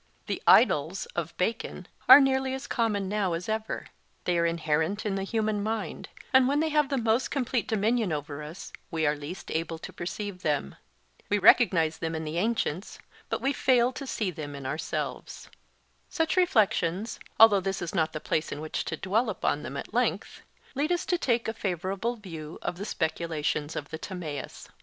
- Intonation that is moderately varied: No, wide, 6.3 semitones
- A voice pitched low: No, high, 195 Hz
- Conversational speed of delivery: Yes, average, 190 wpm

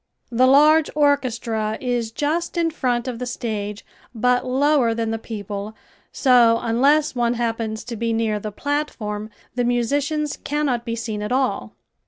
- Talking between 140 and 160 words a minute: Yes, average, 155 wpm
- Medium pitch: No, high, 240 Hz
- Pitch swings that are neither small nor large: Yes, average, 3.9 semitones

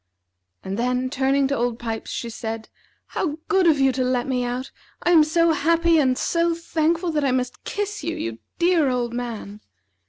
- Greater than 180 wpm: Yes, average, 190 wpm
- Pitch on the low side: No, very high, 270 Hz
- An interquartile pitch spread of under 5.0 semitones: No, average, 5.3 semitones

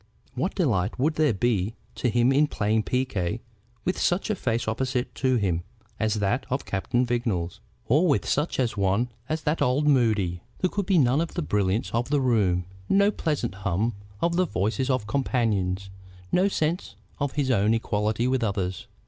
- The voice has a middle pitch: No, low, 120 Hz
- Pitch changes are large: Yes, wide, 5.7 semitones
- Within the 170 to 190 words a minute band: Yes, average, 180 wpm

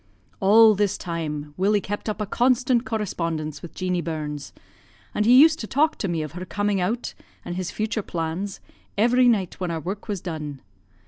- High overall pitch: Yes, high, 195 Hz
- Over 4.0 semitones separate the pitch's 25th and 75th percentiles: Yes, average, 4.7 semitones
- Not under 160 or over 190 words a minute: Yes, average, 185 wpm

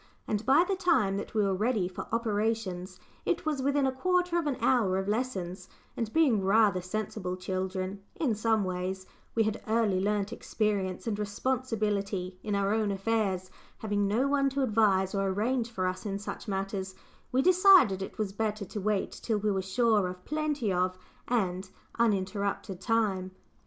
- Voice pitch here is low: No, high, 210 Hz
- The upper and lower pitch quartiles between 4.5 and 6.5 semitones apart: No, average, 3.4 semitones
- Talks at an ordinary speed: Yes, average, 170 wpm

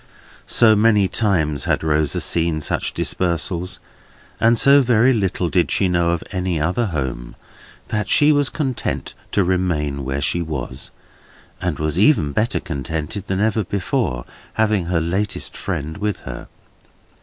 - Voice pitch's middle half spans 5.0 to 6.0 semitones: Yes, wide, 5.4 semitones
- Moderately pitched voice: No, very low, 90 Hz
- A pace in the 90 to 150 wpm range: Yes, average, 145 wpm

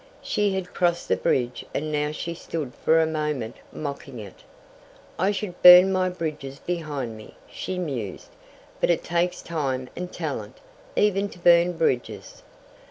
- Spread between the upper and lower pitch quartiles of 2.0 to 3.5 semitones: No, average, 4.7 semitones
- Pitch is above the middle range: No, medium, 160 Hz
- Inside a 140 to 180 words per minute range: Yes, average, 155 wpm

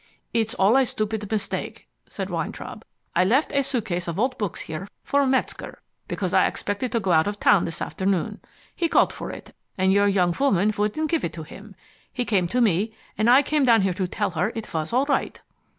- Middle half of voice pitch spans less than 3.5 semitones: No, average, 4.9 semitones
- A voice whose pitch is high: Yes, high, 210 Hz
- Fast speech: Yes, fast, 215 wpm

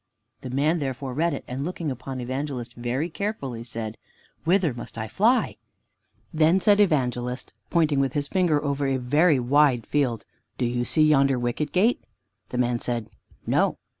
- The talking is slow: No, average, 165 wpm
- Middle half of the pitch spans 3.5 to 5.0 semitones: Yes, average, 4.2 semitones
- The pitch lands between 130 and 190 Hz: Yes, low, 135 Hz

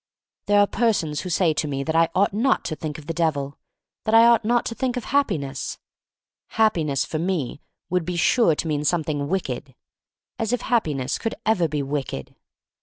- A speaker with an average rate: No, fast, 210 wpm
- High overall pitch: No, medium, 165 Hz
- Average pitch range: No, wide, 6.8 semitones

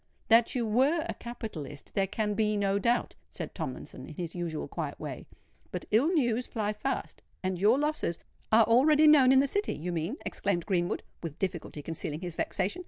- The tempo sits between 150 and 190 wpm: Yes, average, 180 wpm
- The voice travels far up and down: Yes, wide, 6.3 semitones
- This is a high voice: Yes, high, 210 Hz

